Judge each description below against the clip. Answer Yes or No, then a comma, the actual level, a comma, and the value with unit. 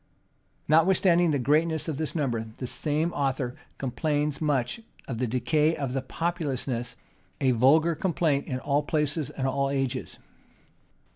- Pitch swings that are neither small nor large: Yes, average, 3.4 semitones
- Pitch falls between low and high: Yes, medium, 145 Hz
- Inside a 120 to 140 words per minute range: Yes, slow, 135 wpm